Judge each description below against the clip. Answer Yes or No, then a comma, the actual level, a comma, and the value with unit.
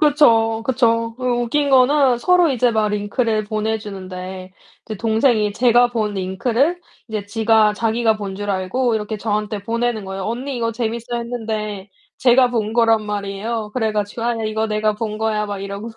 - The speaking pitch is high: Yes, high, 220 Hz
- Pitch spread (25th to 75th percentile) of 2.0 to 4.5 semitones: Yes, narrow, 2.4 semitones